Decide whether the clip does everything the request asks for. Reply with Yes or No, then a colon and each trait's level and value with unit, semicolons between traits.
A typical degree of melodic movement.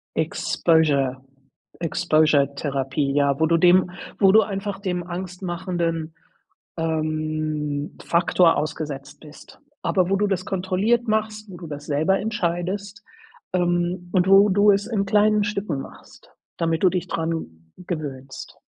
Yes: average, 3.9 semitones